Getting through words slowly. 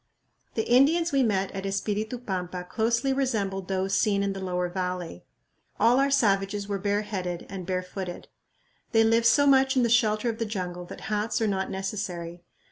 No: average, 175 wpm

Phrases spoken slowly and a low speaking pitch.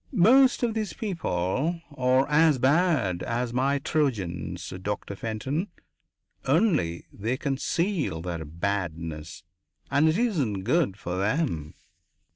Yes: slow, 110 wpm; low, 130 Hz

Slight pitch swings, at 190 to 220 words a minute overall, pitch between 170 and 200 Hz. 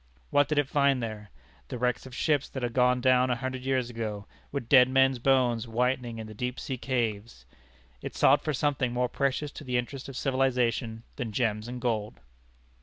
No: narrow, 2.3 semitones; average, 195 wpm; low, 125 Hz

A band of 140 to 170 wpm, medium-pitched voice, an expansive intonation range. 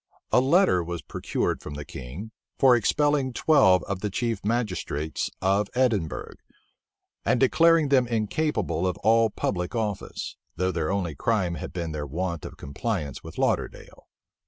No: average, 150 wpm; low, 100 Hz; wide, 6.0 semitones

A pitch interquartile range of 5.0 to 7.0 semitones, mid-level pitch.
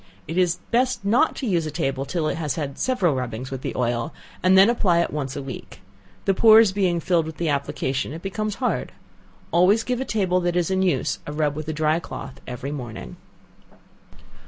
Yes: wide, 5.4 semitones; medium, 170 Hz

